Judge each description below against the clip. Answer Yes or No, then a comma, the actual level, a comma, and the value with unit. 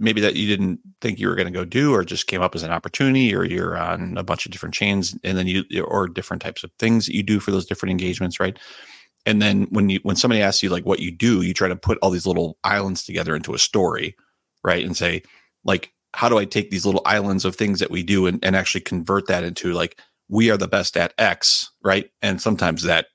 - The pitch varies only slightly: Yes, narrow, 2.2 semitones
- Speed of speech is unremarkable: No, fast, 255 wpm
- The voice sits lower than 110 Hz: Yes, very low, 95 Hz